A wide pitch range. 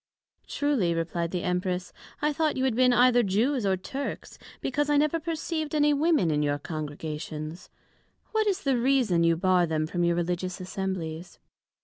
Yes: wide, 8.9 semitones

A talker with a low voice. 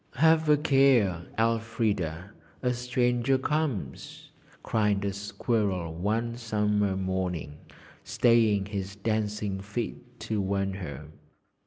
Yes: low, 105 Hz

